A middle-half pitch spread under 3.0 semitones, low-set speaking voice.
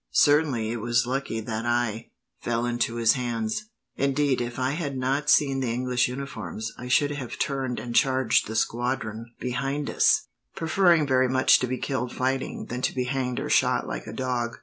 Yes: narrow, 2.6 semitones; low, 125 Hz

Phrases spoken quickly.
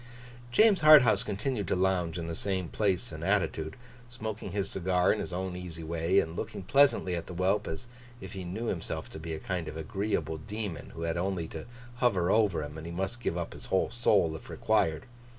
Yes: fast, 210 wpm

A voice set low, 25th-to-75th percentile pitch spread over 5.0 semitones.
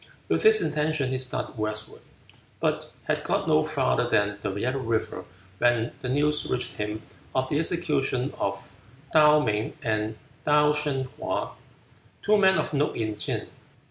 Yes: low, 130 Hz; wide, 5.6 semitones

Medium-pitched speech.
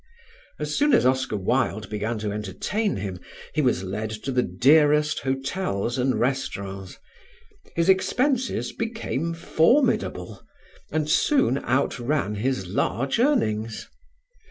No: low, 130 Hz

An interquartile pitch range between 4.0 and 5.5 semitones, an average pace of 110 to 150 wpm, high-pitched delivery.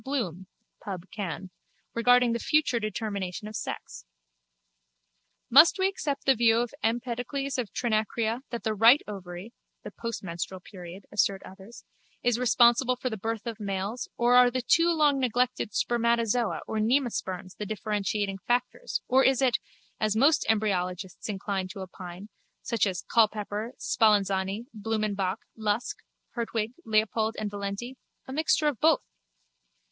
No: average, 3.6 semitones; average, 140 wpm; high, 220 Hz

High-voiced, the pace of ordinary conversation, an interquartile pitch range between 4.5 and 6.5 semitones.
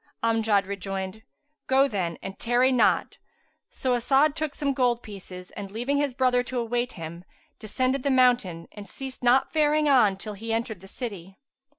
Yes: high, 240 Hz; average, 170 wpm; average, 4.8 semitones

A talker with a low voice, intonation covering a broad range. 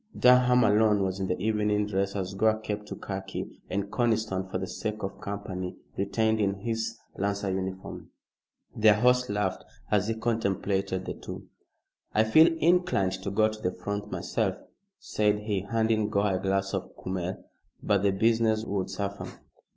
No: low, 105 Hz; narrow, 2.4 semitones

